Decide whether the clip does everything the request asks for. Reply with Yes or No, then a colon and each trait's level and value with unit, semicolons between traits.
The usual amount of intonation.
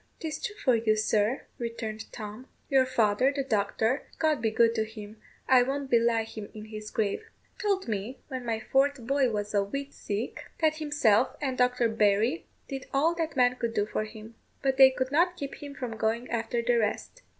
Yes: average, 3.9 semitones